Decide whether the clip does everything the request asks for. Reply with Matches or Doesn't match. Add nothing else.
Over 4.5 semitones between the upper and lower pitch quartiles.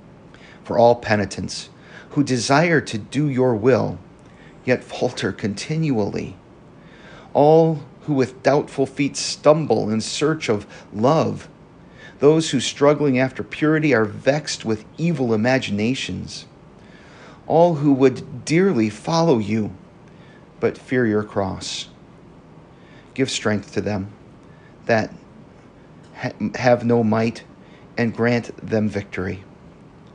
Matches